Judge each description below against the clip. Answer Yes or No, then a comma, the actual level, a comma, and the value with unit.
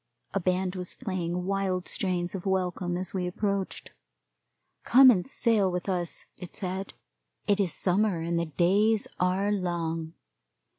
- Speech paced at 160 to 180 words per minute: No, average, 145 wpm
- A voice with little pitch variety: Yes, narrow, 2.0 semitones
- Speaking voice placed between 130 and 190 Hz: Yes, medium, 185 Hz